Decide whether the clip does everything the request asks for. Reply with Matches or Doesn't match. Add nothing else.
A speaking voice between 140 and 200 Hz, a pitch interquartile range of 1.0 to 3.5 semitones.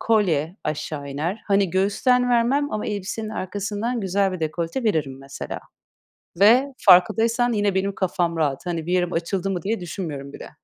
Doesn't match